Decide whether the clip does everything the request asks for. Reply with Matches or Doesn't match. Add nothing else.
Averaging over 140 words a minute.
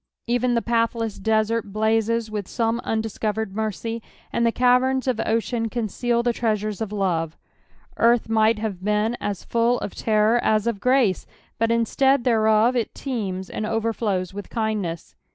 Matches